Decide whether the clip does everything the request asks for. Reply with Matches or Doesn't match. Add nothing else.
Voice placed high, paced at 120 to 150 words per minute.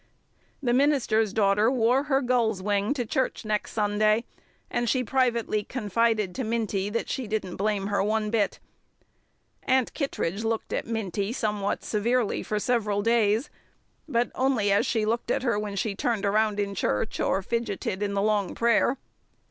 Doesn't match